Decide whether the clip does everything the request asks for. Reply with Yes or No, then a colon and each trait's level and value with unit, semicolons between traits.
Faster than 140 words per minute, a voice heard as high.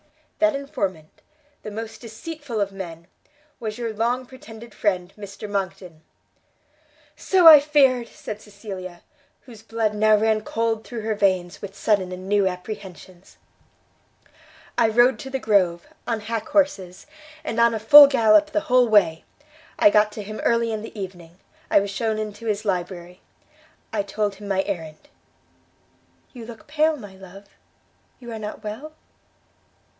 Yes: average, 150 wpm; high, 215 Hz